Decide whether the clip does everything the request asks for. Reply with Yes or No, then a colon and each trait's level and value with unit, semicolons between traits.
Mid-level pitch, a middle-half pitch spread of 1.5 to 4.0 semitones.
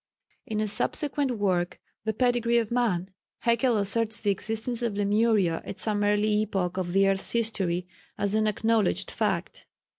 No: high, 215 Hz; average, 2.8 semitones